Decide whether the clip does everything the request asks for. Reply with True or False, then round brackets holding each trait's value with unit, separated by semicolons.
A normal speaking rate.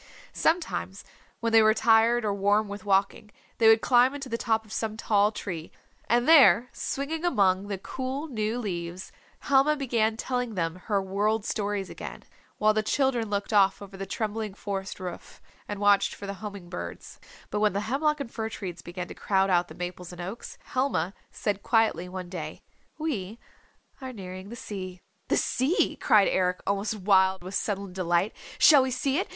True (180 wpm)